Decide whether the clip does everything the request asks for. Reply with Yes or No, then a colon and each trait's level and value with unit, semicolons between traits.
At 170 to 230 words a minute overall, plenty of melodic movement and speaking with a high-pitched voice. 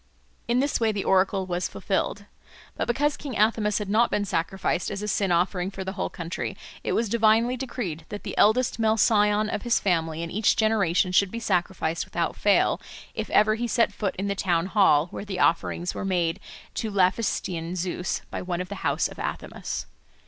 No: average, 200 wpm; average, 3.3 semitones; high, 200 Hz